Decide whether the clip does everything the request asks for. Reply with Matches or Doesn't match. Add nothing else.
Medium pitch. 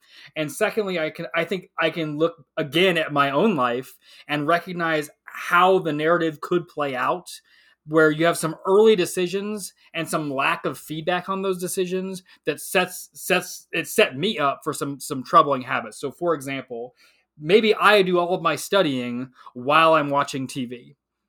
Matches